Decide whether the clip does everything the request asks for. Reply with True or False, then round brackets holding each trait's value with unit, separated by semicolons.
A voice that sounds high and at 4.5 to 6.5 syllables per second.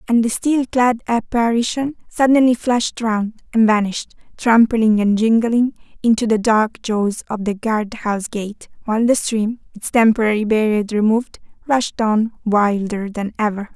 True (225 Hz; 4.6 syllables/s)